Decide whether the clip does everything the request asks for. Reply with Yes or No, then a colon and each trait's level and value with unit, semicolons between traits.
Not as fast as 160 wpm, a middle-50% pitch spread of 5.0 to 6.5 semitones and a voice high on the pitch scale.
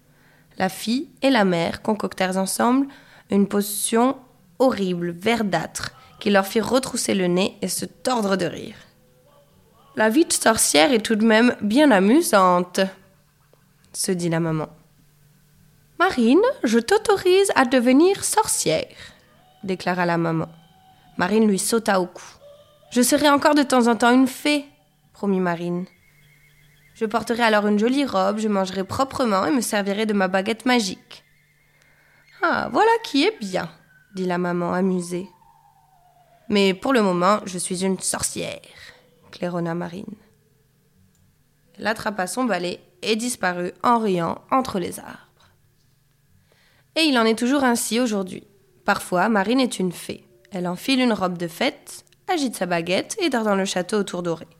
Yes: average, 150 wpm; wide, 5.6 semitones; high, 195 Hz